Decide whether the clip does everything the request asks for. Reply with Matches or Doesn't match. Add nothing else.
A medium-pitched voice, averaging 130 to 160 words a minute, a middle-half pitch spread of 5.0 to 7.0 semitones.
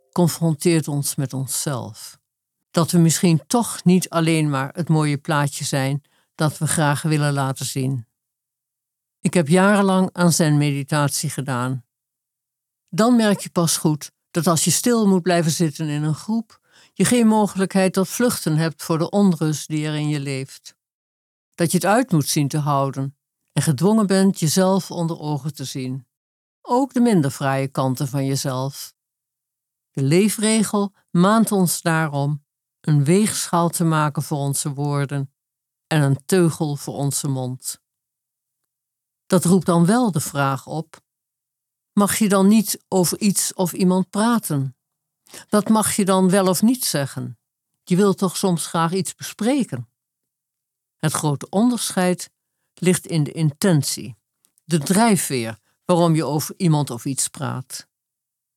Matches